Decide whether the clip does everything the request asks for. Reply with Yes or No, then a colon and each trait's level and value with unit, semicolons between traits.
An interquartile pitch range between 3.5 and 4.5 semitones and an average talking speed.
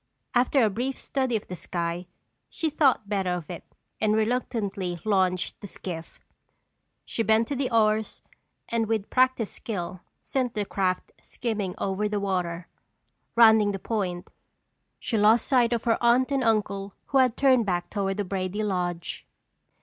Yes: average, 4.1 semitones; average, 155 wpm